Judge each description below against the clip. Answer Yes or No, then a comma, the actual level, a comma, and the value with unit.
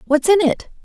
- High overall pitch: Yes, very high, 315 Hz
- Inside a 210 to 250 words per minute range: Yes, fast, 215 wpm